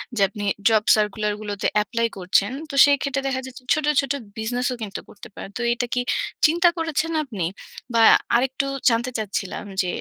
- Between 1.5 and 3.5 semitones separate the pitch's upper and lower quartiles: No, average, 4.4 semitones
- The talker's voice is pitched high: Yes, high, 240 Hz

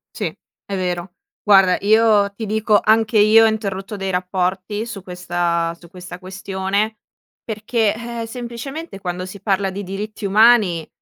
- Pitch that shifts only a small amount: No, average, 3.0 semitones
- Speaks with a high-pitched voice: Yes, high, 200 Hz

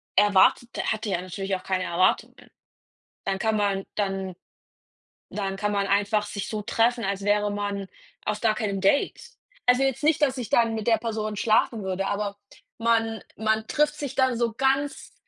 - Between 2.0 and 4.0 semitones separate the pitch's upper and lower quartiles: Yes, average, 2.7 semitones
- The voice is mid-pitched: No, high, 210 Hz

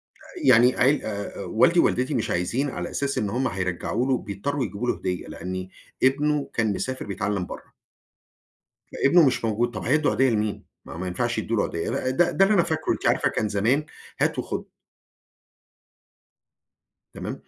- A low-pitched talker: Yes, low, 120 Hz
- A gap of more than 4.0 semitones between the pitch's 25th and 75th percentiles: Yes, average, 5.2 semitones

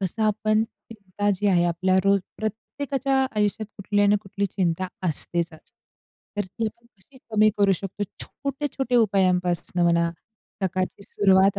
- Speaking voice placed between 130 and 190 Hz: No, high, 200 Hz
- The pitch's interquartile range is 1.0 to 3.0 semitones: Yes, average, 2.7 semitones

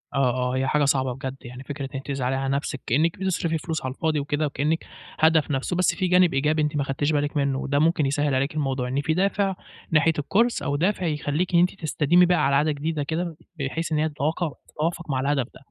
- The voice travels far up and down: No, average, 3.0 semitones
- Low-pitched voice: No, medium, 150 Hz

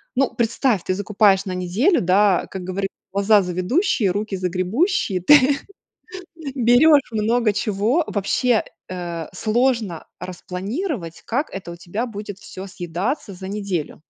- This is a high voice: Yes, high, 205 Hz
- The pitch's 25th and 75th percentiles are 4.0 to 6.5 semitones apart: Yes, average, 4.8 semitones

